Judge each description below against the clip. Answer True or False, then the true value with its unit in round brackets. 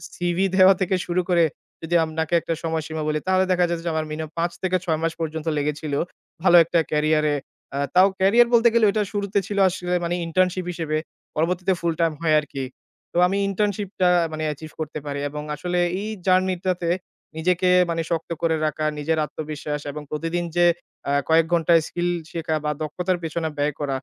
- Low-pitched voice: False (165 Hz)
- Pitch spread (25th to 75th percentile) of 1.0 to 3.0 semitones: True (2.7 semitones)